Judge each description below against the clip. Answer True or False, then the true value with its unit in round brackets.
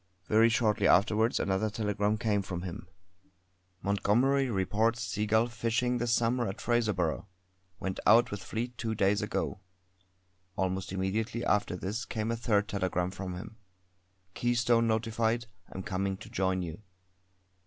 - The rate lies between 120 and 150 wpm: True (135 wpm)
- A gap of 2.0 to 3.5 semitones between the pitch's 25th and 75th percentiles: True (3.2 semitones)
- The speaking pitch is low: True (105 Hz)